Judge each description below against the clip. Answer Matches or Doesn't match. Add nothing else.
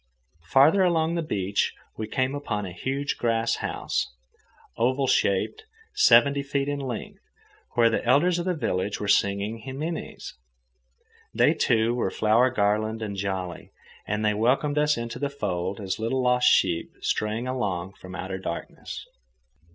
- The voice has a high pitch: Doesn't match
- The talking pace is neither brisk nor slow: Matches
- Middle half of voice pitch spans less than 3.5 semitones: Doesn't match